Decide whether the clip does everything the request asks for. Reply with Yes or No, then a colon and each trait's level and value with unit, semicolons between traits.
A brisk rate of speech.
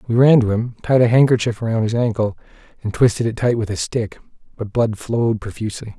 Yes: fast, 210 wpm